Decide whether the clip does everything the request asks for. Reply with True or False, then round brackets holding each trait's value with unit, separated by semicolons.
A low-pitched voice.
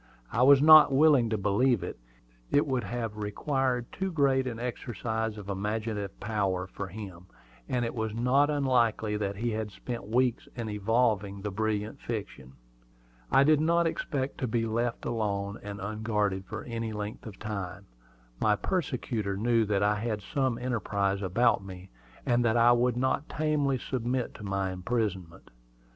True (110 Hz)